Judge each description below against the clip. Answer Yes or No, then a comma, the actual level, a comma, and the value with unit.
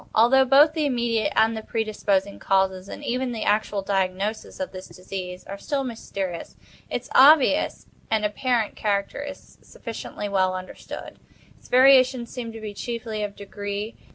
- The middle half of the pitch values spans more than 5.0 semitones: No, average, 4.0 semitones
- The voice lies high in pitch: Yes, high, 220 Hz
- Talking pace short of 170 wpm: Yes, average, 155 wpm